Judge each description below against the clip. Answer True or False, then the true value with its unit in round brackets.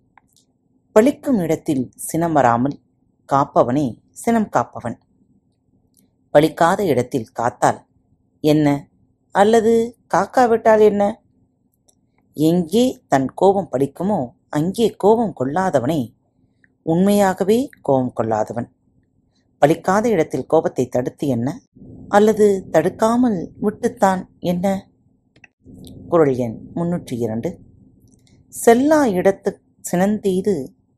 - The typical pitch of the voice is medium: True (180 Hz)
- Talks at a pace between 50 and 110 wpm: True (75 wpm)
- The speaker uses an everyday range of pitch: False (7.8 semitones)